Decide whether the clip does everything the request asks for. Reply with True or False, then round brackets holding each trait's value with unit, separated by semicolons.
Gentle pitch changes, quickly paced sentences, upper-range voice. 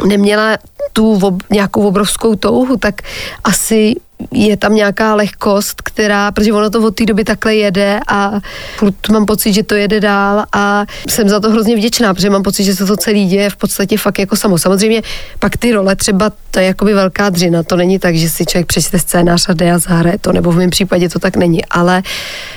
True (2.2 semitones; 205 wpm; 205 Hz)